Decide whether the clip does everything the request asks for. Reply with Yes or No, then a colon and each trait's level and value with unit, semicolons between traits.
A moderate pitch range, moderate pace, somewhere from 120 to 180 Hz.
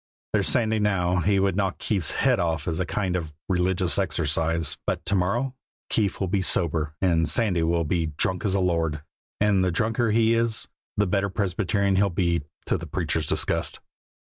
No: average, 3.2 semitones; average, 185 wpm; very low, 90 Hz